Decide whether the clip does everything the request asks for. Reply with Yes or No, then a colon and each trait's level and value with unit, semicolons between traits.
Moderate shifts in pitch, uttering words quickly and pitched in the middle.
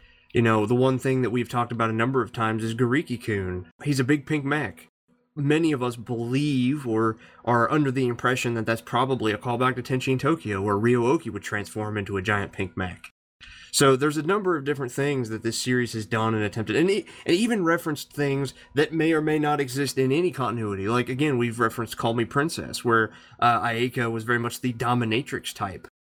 No: average, 3.6 semitones; fast, 210 wpm; low, 120 Hz